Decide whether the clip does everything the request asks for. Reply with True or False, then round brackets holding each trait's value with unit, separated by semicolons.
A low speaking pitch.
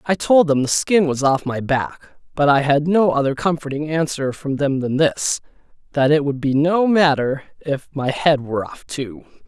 False (145 Hz)